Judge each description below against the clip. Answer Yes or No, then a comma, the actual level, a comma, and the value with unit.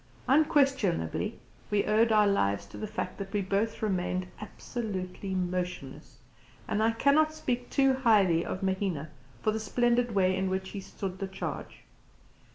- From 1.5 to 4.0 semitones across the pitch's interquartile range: Yes, average, 3.7 semitones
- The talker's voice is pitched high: Yes, high, 200 Hz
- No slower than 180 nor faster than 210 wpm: No, average, 155 wpm